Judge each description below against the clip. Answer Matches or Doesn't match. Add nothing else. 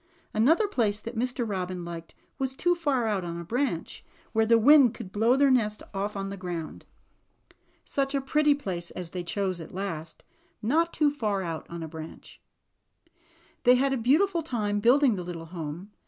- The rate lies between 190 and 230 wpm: Matches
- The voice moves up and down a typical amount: Doesn't match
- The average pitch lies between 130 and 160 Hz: Doesn't match